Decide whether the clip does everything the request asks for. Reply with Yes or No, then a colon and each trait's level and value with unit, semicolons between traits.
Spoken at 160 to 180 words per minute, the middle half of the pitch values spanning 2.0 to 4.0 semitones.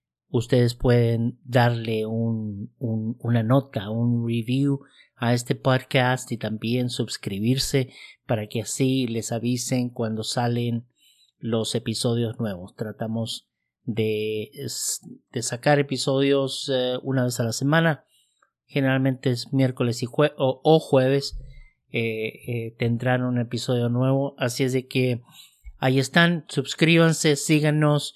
No: slow, 125 wpm; average, 2.7 semitones